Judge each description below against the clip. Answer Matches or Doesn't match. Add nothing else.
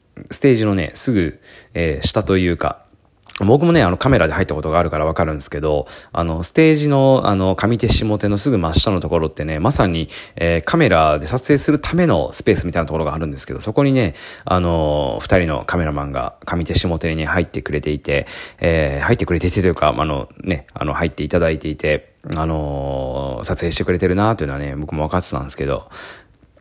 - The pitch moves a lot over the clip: Doesn't match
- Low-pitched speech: Matches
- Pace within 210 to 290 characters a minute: Doesn't match